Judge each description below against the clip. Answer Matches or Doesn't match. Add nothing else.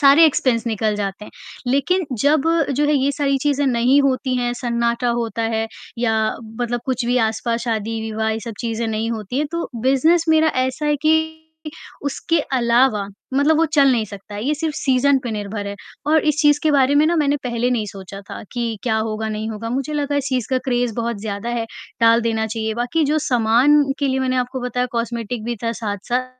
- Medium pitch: Doesn't match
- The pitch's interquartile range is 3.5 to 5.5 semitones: Matches